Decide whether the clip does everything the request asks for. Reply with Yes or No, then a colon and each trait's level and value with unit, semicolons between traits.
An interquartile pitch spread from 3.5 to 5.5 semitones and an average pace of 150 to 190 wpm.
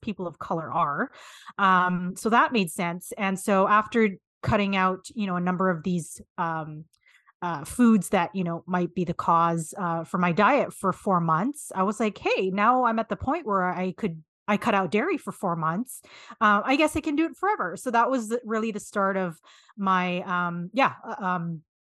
No: average, 3.8 semitones; fast, 205 wpm